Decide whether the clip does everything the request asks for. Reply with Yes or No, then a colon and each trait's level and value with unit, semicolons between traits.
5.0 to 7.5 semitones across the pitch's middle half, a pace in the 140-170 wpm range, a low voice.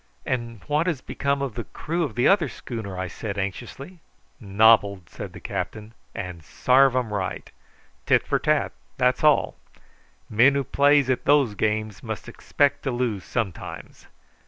Yes: average, 5.3 semitones; average, 160 wpm; low, 120 Hz